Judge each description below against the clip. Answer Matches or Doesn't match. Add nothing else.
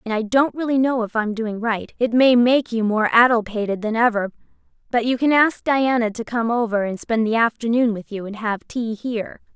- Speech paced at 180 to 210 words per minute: Matches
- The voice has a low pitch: Doesn't match